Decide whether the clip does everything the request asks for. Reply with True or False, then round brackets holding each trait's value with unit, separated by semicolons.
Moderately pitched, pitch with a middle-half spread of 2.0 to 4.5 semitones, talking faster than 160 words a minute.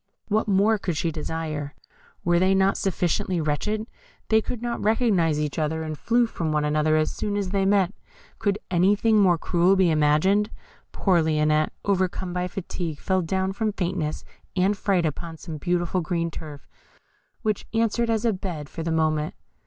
True (180 Hz; 4.2 semitones; 170 wpm)